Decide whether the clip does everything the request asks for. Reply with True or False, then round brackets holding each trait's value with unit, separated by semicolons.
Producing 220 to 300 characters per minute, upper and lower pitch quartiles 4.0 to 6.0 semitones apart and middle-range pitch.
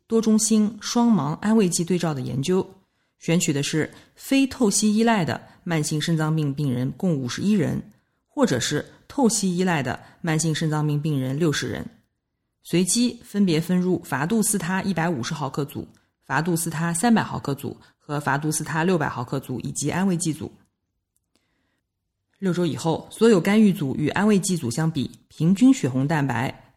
True (260 characters per minute; 5.4 semitones; 165 Hz)